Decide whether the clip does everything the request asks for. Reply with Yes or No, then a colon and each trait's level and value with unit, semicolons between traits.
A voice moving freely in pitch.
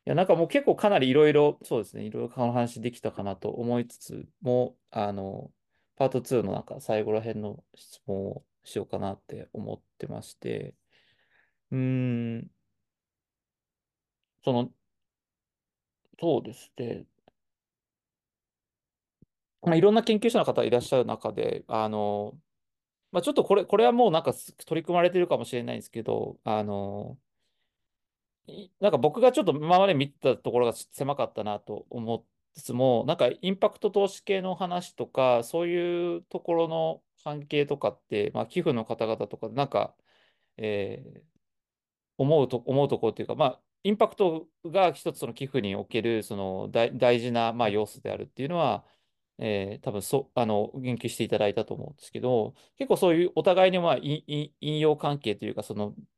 Yes: wide, 7.5 semitones